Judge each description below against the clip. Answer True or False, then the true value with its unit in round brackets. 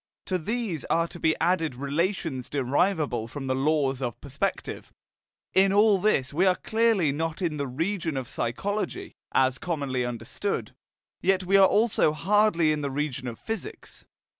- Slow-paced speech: False (160 wpm)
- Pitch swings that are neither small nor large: False (6.1 semitones)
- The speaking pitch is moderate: True (160 Hz)